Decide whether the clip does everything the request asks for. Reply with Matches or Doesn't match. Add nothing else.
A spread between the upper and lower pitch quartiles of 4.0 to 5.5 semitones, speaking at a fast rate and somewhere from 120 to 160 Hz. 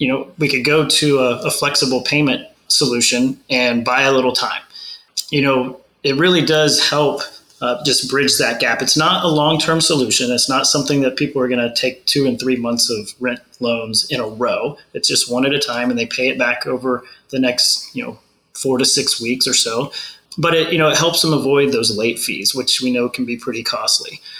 Doesn't match